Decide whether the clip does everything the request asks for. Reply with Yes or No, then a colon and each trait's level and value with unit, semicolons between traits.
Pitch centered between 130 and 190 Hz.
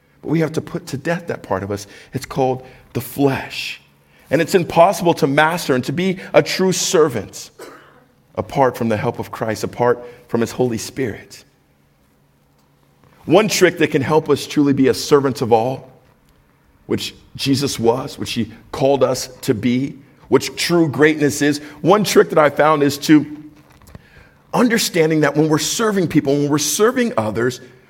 Yes: medium, 140 Hz